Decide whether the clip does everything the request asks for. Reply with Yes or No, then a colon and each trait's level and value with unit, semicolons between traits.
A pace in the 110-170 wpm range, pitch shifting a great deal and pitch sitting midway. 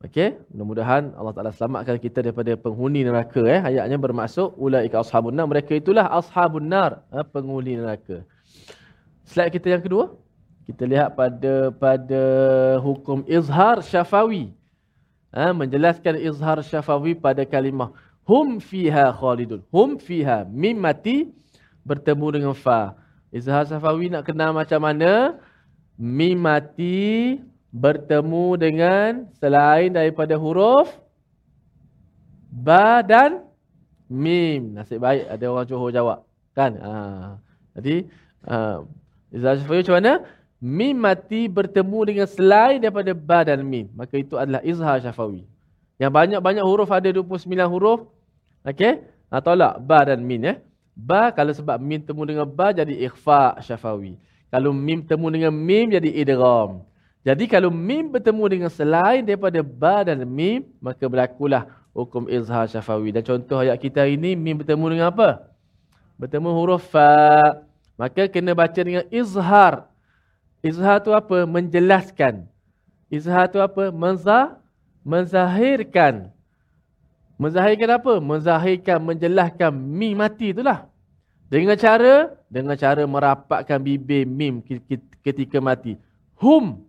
Yes: fast, 125 wpm; wide, 6.1 semitones; medium, 150 Hz